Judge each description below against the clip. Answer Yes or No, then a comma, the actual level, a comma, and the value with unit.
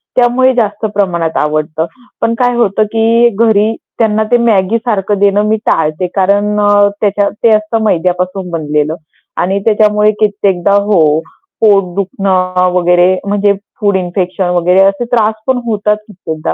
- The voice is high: Yes, high, 200 Hz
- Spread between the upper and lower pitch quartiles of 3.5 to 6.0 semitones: No, average, 2.9 semitones